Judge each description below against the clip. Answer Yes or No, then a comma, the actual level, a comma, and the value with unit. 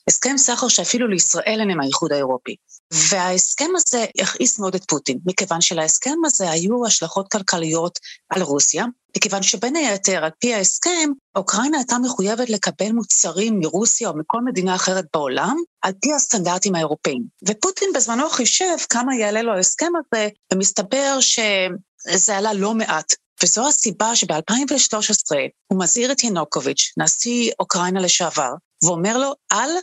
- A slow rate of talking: No, average, 135 wpm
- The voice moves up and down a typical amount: Yes, average, 4.9 semitones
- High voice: Yes, high, 210 Hz